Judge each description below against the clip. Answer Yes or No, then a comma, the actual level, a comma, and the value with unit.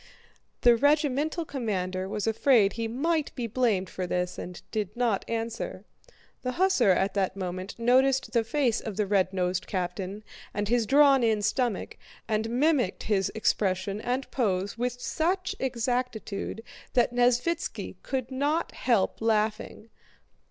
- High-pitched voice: Yes, high, 230 Hz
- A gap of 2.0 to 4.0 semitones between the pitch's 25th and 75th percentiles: No, average, 4.6 semitones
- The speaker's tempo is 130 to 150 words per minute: Yes, average, 140 wpm